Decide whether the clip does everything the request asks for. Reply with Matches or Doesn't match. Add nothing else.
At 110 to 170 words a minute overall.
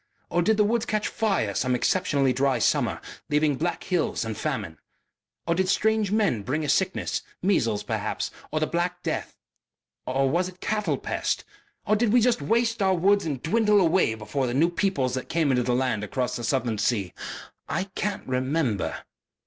Doesn't match